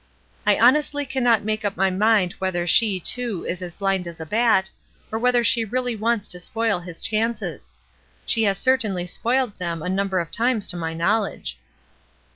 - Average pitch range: Yes, average, 4.3 semitones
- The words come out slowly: No, average, 180 wpm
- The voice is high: Yes, high, 210 Hz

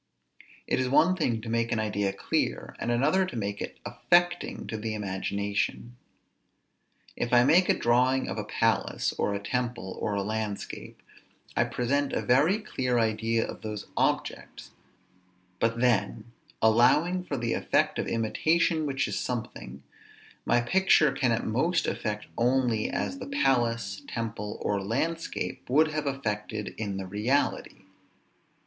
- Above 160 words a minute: No, average, 150 wpm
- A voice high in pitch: No, low, 120 Hz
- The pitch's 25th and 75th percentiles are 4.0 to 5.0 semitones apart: Yes, average, 4.6 semitones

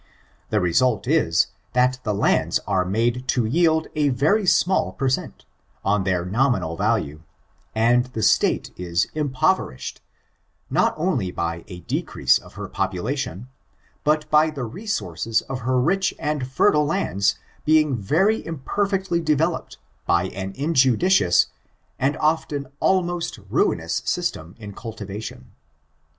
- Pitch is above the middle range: No, low, 130 Hz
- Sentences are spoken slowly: Yes, slow, 130 wpm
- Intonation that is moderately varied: No, wide, 7.8 semitones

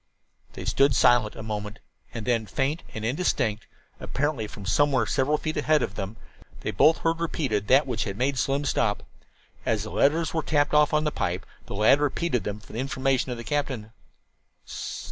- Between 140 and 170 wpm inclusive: No, average, 185 wpm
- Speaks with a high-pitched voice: No, low, 130 Hz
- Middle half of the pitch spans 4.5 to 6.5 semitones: Yes, average, 5.3 semitones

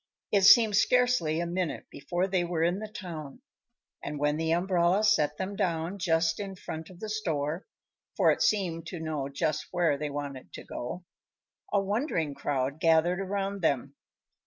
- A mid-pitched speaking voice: Yes, medium, 170 Hz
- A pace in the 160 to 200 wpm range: Yes, average, 170 wpm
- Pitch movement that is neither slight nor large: Yes, average, 4.1 semitones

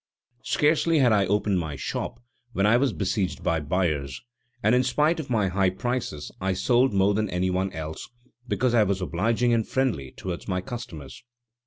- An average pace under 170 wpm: No, average, 180 wpm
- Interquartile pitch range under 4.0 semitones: No, average, 5.0 semitones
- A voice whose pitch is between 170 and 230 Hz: No, low, 100 Hz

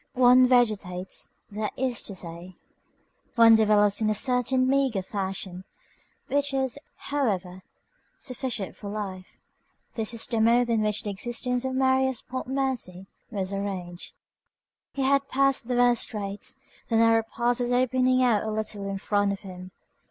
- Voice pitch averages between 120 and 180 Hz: No, high, 225 Hz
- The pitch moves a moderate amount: Yes, average, 4.2 semitones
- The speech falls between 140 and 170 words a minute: Yes, average, 150 wpm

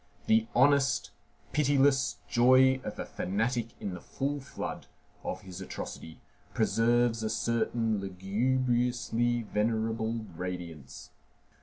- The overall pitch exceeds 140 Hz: No, low, 115 Hz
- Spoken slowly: Yes, slow, 105 wpm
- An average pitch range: Yes, average, 3.8 semitones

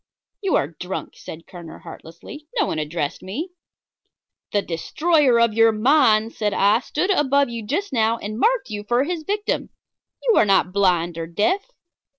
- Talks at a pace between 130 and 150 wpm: No, average, 165 wpm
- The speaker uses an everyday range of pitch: No, wide, 8.0 semitones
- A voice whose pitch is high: Yes, high, 225 Hz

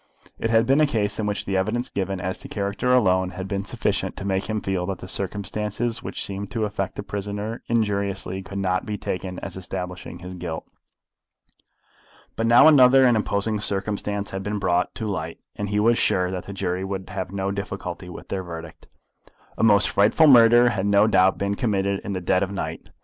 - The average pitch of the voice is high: No, low, 100 Hz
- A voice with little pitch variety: Yes, narrow, 2.2 semitones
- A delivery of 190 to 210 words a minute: Yes, fast, 205 wpm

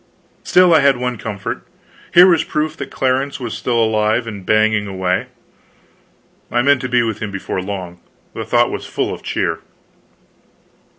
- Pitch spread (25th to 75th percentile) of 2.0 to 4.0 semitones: No, average, 4.7 semitones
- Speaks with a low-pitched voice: Yes, low, 115 Hz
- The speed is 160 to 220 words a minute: Yes, average, 165 wpm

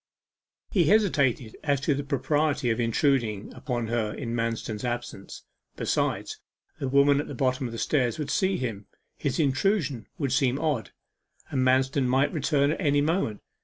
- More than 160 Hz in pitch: No, low, 135 Hz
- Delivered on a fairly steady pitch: No, average, 3.3 semitones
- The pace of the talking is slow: No, average, 165 wpm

